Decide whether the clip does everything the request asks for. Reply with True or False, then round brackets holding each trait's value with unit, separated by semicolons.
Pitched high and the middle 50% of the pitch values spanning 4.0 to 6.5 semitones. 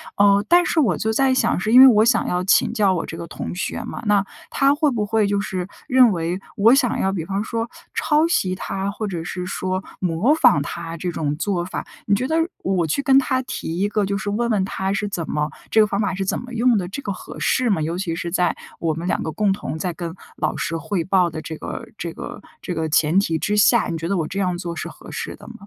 True (195 Hz; 4.5 semitones)